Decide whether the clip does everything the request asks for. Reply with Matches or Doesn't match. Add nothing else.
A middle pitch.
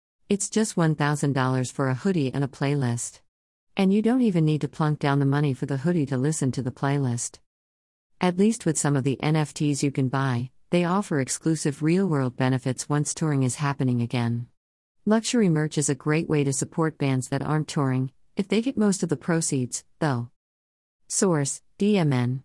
Matches